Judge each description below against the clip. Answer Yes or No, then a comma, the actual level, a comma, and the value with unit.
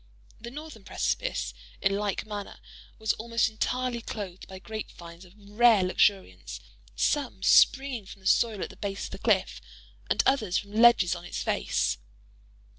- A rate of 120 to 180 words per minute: Yes, average, 160 wpm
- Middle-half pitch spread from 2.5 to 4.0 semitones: Yes, average, 3.7 semitones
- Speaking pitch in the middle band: No, high, 210 Hz